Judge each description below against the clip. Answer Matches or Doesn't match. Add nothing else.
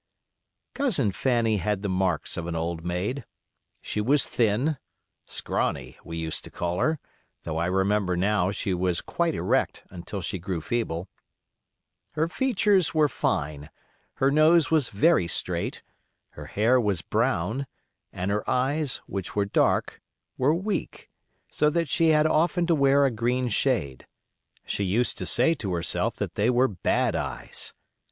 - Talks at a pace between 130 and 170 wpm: Matches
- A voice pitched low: Matches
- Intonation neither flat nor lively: Doesn't match